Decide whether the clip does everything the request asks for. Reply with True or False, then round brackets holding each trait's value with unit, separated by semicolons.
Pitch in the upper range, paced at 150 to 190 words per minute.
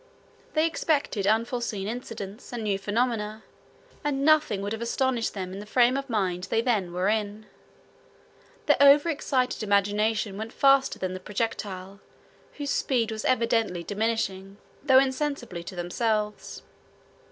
False (220 Hz; 135 wpm)